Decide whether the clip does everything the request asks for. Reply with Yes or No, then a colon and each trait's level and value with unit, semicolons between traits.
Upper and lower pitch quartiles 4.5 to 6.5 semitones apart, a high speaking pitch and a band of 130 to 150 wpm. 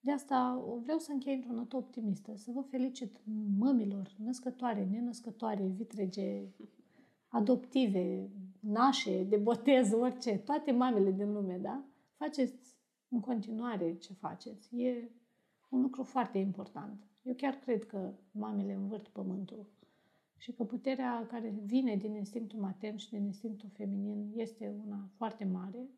No: average, 3.7 semitones; high, 225 Hz; average, 135 wpm